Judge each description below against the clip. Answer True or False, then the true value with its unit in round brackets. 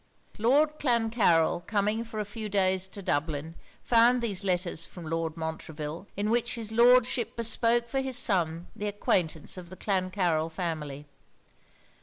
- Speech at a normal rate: True (145 wpm)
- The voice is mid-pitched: False (200 Hz)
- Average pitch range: False (5.8 semitones)